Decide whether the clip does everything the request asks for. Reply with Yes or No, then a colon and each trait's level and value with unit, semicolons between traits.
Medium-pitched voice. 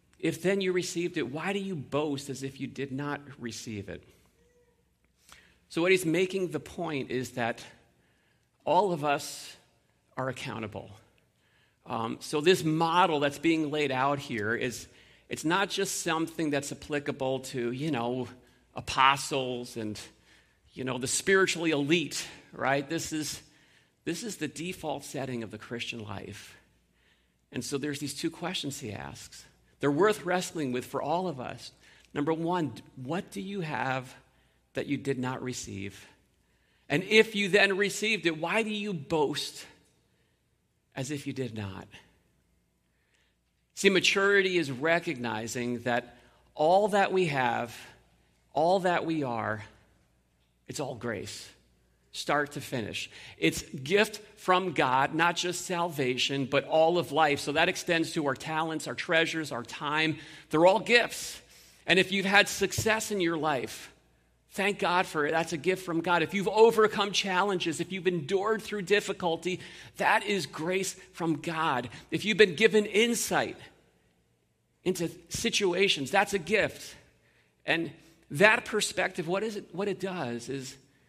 Yes: medium, 155 Hz